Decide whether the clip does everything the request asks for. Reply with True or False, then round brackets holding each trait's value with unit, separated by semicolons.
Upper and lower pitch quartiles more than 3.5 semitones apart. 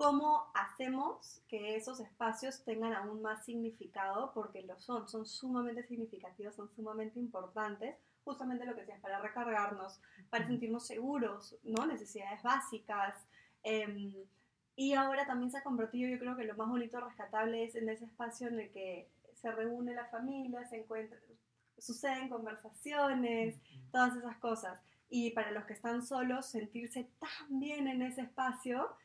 False (2.7 semitones)